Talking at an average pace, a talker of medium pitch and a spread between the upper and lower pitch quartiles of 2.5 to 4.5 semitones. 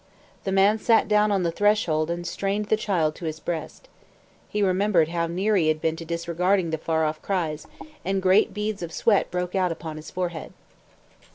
Yes: average, 195 wpm; medium, 180 Hz; average, 3.7 semitones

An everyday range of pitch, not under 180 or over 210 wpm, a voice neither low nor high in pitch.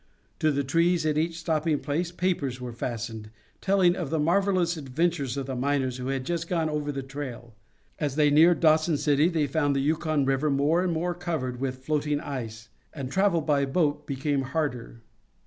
Yes: average, 3.6 semitones; average, 185 wpm; medium, 150 Hz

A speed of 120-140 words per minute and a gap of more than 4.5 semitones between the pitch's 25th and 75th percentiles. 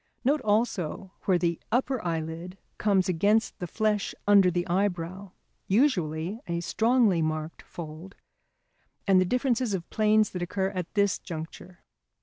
No: slow, 135 wpm; average, 3.9 semitones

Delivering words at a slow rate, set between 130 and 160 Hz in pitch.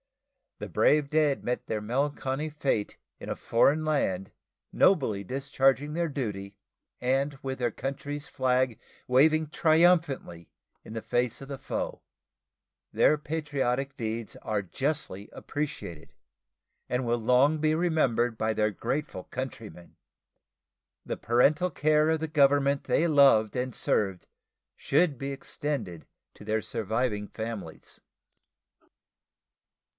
Yes: slow, 120 wpm; low, 135 Hz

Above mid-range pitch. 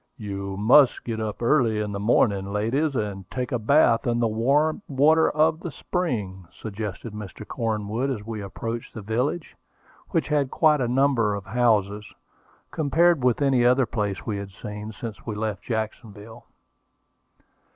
No: low, 115 Hz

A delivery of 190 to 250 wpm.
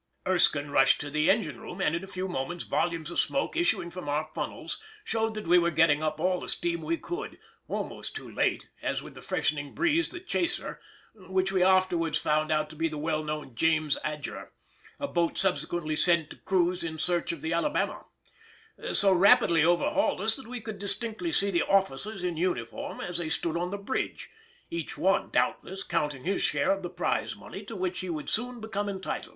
Yes: average, 200 wpm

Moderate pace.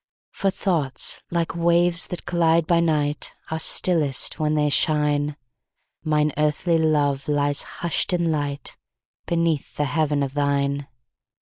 No: slow, 115 wpm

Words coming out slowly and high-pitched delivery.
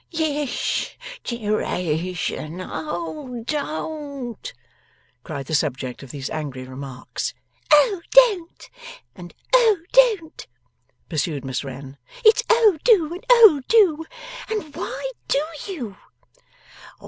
Yes: slow, 100 wpm; very high, 270 Hz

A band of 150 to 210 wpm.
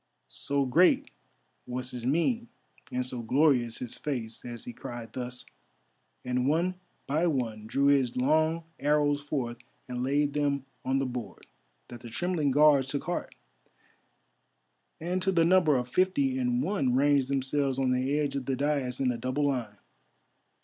Yes: average, 160 wpm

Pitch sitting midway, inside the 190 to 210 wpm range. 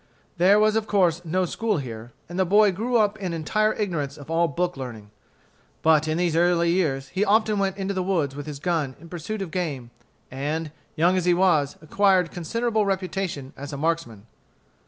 Yes: medium, 175 Hz; average, 195 wpm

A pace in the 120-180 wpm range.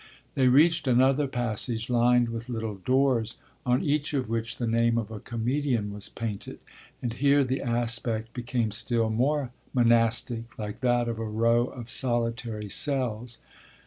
Yes: average, 150 wpm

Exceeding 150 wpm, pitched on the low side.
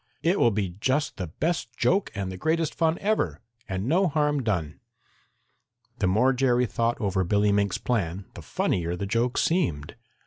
Yes: average, 170 wpm; low, 115 Hz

